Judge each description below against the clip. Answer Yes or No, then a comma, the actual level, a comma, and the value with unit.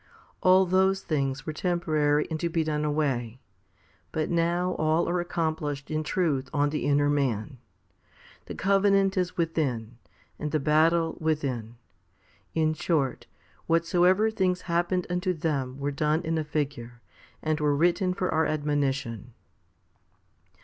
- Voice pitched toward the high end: No, medium, 155 Hz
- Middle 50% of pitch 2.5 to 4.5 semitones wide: Yes, average, 3.3 semitones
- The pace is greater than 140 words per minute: No, slow, 135 wpm